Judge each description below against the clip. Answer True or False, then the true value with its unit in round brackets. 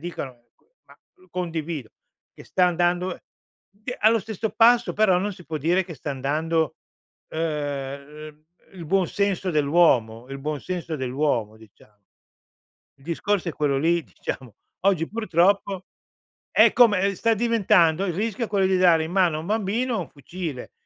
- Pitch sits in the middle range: True (170 Hz)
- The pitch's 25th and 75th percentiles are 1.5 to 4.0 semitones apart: False (4.6 semitones)